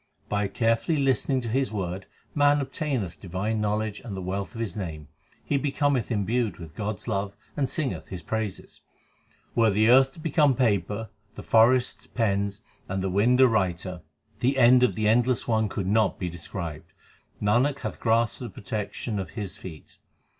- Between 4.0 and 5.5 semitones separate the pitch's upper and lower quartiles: Yes, average, 4.4 semitones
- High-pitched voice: No, low, 110 Hz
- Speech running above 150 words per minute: Yes, average, 175 wpm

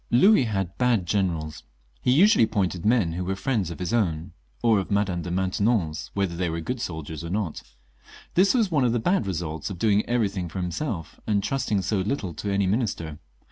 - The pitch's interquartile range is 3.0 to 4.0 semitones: No, average, 5.0 semitones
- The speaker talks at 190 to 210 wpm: Yes, average, 200 wpm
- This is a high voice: No, low, 100 Hz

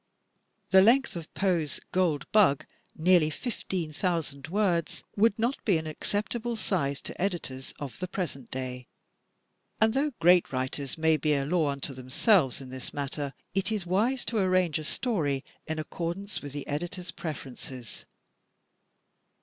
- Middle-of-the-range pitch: Yes, medium, 165 Hz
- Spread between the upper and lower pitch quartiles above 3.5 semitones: Yes, wide, 5.5 semitones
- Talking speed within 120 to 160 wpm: Yes, average, 150 wpm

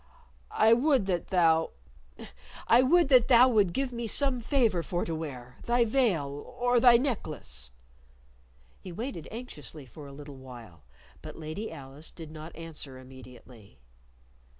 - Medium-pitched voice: Yes, medium, 170 Hz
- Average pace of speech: Yes, average, 145 wpm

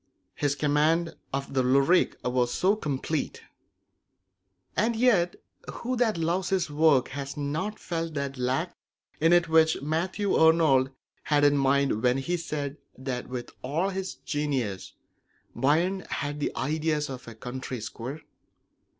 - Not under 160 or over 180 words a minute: No, average, 140 wpm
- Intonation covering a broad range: No, average, 3.9 semitones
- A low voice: No, medium, 150 Hz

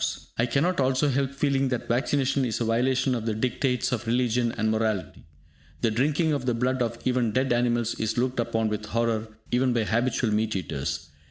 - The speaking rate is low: No, average, 190 wpm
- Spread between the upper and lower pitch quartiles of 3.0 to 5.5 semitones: No, narrow, 2.6 semitones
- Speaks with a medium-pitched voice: No, low, 120 Hz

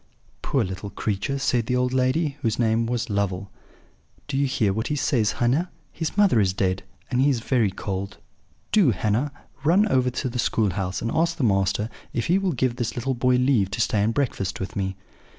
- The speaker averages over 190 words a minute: Yes, fast, 205 wpm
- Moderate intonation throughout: Yes, average, 4.9 semitones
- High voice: No, low, 120 Hz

